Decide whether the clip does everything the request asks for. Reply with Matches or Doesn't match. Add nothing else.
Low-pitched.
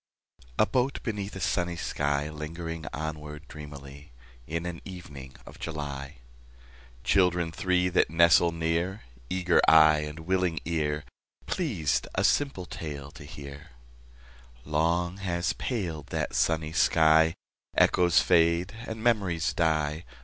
Matches